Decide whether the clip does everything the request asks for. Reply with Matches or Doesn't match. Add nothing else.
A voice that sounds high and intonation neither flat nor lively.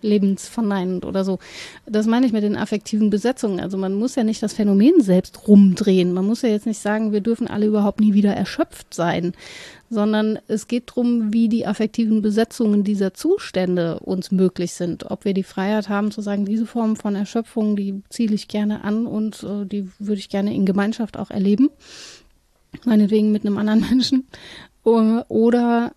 Doesn't match